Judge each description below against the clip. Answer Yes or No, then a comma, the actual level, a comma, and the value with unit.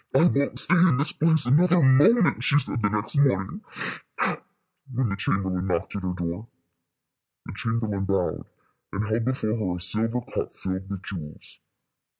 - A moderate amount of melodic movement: No, wide, 6.2 semitones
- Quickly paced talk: No, average, 160 wpm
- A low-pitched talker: Yes, low, 110 Hz